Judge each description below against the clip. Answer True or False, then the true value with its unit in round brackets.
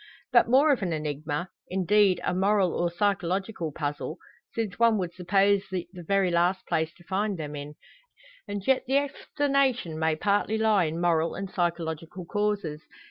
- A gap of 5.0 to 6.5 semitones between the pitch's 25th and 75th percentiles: False (3.9 semitones)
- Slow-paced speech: False (165 wpm)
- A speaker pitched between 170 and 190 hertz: True (185 Hz)